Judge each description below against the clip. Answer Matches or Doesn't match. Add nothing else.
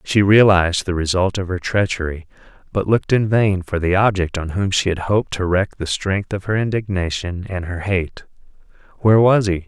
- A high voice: Doesn't match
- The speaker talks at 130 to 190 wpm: Doesn't match